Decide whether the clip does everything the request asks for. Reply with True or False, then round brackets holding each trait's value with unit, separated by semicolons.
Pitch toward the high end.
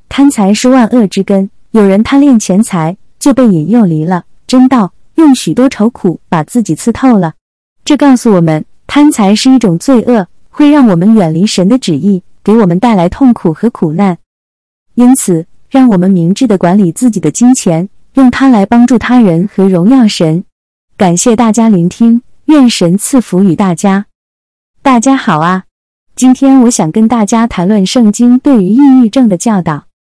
True (215 Hz)